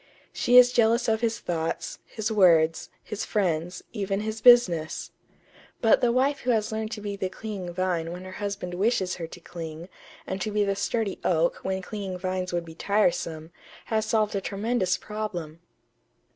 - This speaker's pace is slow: No, average, 175 wpm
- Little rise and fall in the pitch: No, average, 3.6 semitones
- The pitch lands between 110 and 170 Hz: No, high, 195 Hz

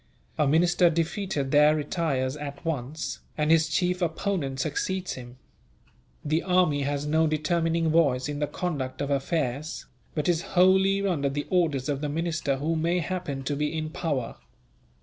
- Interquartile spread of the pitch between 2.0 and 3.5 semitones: Yes, average, 3.2 semitones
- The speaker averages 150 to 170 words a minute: Yes, average, 160 wpm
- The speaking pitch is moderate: Yes, medium, 155 Hz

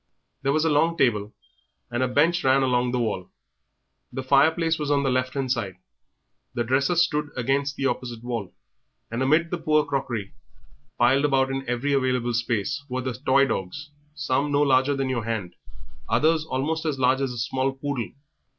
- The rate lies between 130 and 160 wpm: No, average, 180 wpm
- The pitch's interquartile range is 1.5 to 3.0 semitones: Yes, average, 2.7 semitones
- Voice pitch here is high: No, low, 135 Hz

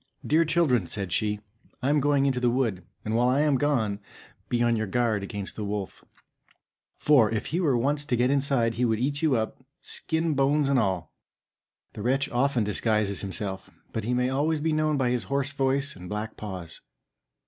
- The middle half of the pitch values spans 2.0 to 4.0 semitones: No, average, 4.6 semitones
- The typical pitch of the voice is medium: No, low, 125 Hz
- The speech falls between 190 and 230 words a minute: Yes, average, 200 wpm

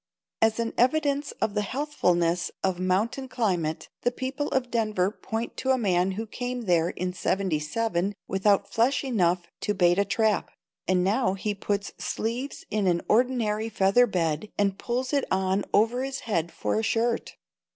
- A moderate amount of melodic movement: Yes, average, 4.7 semitones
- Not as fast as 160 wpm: No, average, 165 wpm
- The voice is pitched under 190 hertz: No, high, 210 Hz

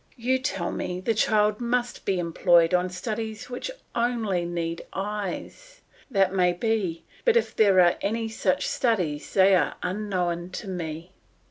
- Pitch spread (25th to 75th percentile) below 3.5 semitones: No, average, 4.0 semitones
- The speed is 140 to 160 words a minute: Yes, average, 150 wpm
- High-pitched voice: Yes, high, 195 Hz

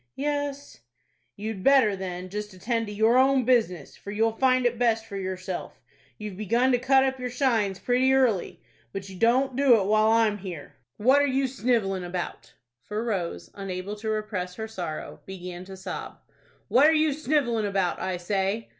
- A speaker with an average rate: Yes, average, 175 wpm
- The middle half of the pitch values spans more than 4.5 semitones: Yes, average, 5.0 semitones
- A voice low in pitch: No, high, 220 Hz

